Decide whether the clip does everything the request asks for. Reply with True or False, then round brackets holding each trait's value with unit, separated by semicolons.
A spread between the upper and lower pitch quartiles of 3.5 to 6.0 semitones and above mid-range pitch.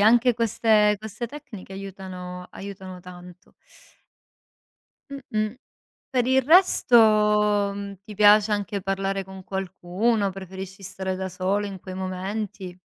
False (2.4 semitones; 195 Hz)